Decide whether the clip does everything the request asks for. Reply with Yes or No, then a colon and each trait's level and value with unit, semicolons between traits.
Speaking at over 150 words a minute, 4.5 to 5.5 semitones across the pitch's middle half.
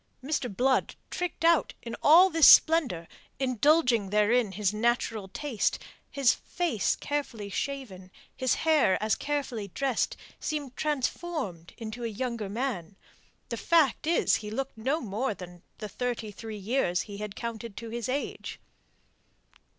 No: slow, 135 wpm; average, 5.1 semitones